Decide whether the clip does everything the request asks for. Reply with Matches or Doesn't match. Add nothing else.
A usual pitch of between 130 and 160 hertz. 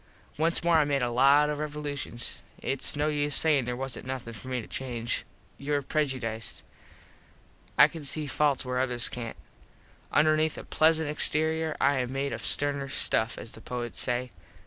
Matches